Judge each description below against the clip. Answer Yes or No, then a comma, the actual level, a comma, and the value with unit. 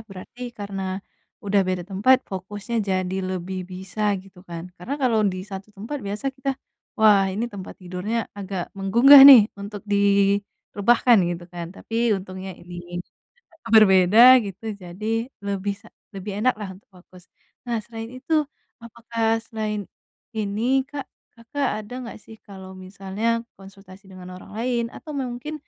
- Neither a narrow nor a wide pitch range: Yes, average, 3.5 semitones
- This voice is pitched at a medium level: No, high, 205 Hz